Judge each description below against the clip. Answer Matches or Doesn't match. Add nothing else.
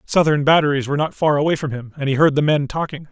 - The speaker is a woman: Doesn't match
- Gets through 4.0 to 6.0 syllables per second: Doesn't match